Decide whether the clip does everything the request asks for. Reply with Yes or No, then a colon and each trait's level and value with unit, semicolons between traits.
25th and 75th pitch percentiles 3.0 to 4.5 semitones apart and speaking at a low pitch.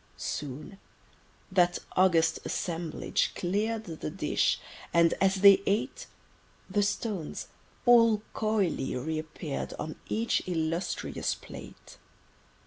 No: average, 4.2 semitones; medium, 185 Hz